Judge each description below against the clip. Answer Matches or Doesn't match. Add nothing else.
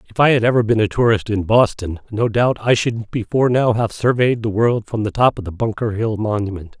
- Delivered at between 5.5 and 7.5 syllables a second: Matches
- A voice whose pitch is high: Doesn't match